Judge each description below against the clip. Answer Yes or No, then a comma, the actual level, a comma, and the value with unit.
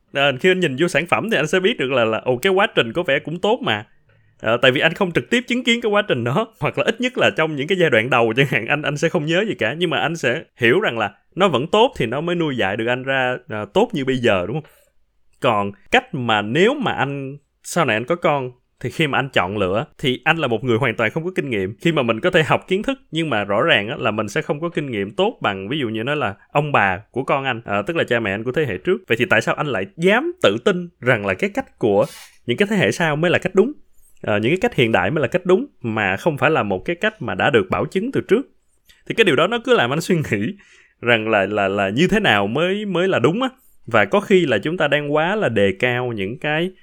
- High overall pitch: No, medium, 150 Hz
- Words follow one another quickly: Yes, fast, 295 wpm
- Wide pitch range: Yes, wide, 7.8 semitones